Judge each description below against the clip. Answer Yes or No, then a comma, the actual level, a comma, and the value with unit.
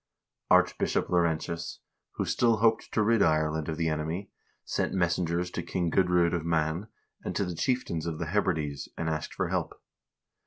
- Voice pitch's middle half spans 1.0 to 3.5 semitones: Yes, average, 2.7 semitones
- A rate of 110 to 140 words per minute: No, average, 170 wpm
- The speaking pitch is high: No, very low, 85 Hz